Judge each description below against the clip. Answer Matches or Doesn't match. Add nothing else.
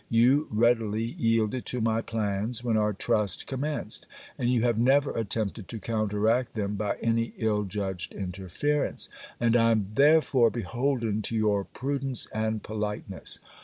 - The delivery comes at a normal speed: Matches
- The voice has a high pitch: Doesn't match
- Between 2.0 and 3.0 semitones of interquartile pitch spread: Matches